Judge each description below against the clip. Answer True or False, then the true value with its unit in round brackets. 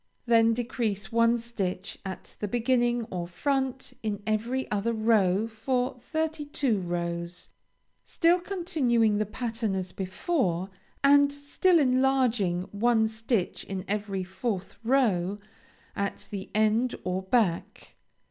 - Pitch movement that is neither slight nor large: True (4.7 semitones)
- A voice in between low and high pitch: False (225 Hz)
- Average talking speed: False (120 wpm)